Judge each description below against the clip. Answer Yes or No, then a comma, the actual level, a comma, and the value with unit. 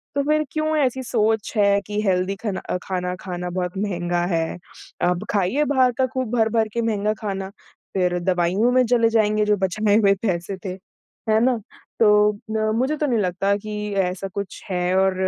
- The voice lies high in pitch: Yes, high, 205 Hz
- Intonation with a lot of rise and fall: No, average, 3.8 semitones